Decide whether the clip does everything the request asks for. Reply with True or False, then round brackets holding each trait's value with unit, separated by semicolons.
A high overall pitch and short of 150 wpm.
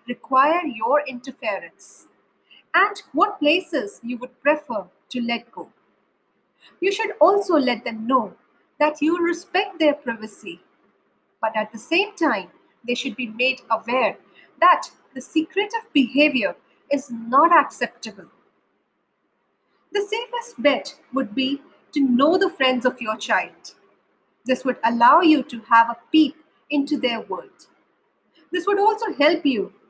True (285 Hz; 140 wpm)